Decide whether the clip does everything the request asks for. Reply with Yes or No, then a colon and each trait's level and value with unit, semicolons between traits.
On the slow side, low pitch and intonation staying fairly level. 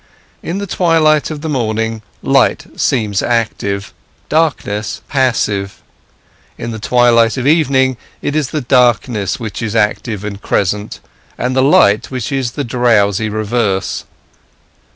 No: slow, 130 wpm; low, 115 Hz; average, 4.2 semitones